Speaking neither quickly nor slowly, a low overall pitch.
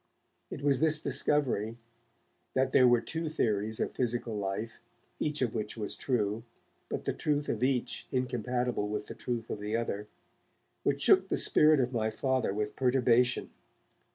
Yes: average, 160 wpm; low, 120 Hz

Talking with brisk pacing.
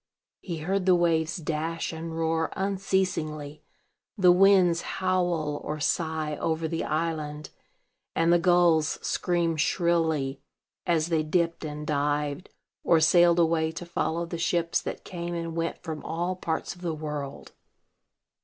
No: average, 140 wpm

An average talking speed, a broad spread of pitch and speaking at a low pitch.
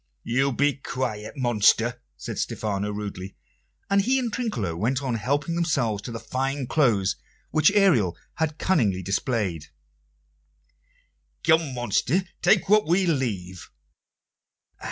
No: slow, 120 wpm; wide, 7.3 semitones; low, 125 Hz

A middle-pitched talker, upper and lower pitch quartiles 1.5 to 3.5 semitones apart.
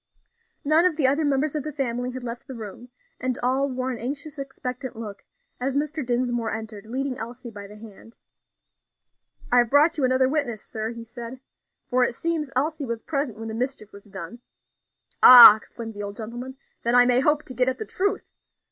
No: very high, 250 Hz; average, 3.2 semitones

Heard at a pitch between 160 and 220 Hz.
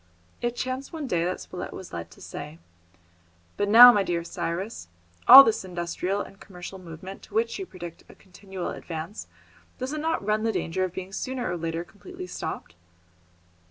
Yes: high, 190 Hz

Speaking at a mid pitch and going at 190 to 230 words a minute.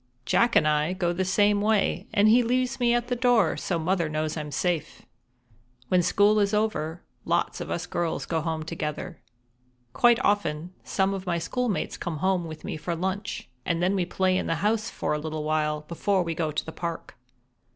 Yes: medium, 180 Hz; average, 200 wpm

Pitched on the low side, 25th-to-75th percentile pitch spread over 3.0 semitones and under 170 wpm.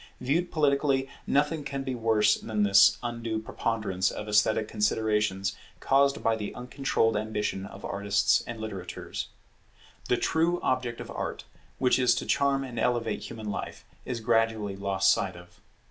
Yes: low, 115 Hz; average, 3.8 semitones; average, 150 wpm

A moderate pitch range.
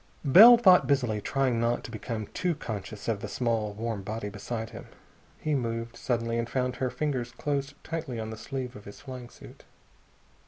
Yes: average, 3.4 semitones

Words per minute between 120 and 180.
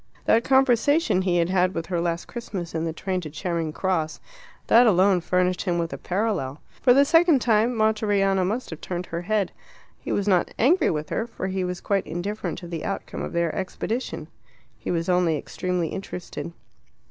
No: average, 190 wpm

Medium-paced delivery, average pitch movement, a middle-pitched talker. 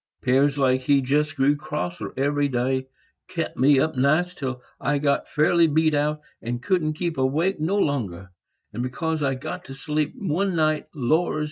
Yes: average, 170 wpm; average, 3.0 semitones; medium, 145 Hz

